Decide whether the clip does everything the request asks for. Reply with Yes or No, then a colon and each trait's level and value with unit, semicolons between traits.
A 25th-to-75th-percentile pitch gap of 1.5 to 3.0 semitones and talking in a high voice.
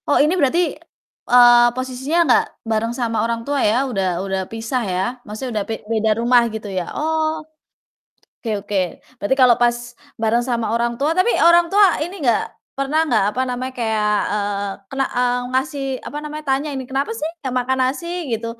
No: average, 3.6 semitones; high, 245 Hz